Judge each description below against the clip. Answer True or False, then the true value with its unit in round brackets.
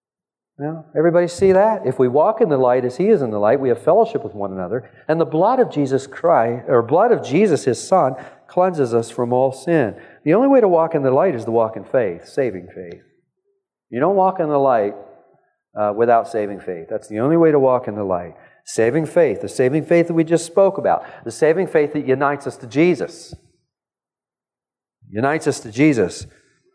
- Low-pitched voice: False (145 Hz)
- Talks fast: True (215 wpm)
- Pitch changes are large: True (6.3 semitones)